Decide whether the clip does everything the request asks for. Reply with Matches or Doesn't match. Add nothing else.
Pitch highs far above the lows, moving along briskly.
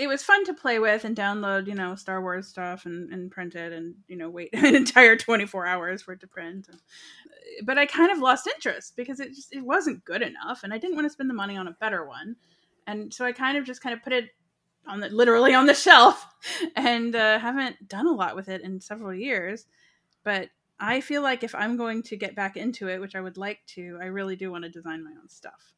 Matches